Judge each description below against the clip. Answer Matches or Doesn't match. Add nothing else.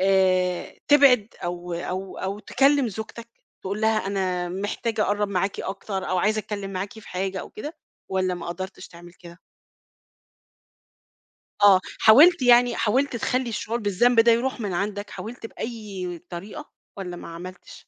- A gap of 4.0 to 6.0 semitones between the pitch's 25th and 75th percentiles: Doesn't match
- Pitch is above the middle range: Matches